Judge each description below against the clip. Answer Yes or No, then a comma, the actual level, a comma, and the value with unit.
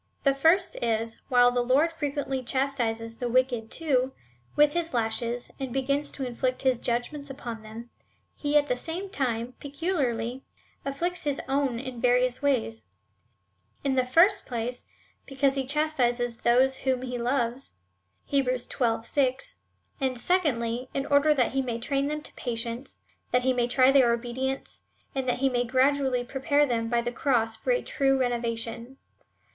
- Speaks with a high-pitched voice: Yes, very high, 255 Hz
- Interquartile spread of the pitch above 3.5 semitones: No, average, 2.7 semitones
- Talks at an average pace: Yes, average, 170 wpm